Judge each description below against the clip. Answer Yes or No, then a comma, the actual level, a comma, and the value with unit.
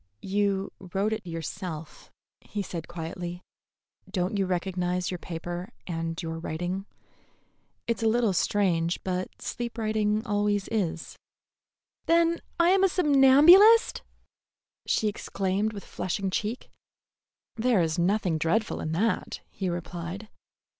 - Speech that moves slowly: Yes, slow, 120 wpm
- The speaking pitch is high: Yes, high, 195 Hz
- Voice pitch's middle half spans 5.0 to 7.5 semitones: No, average, 3.9 semitones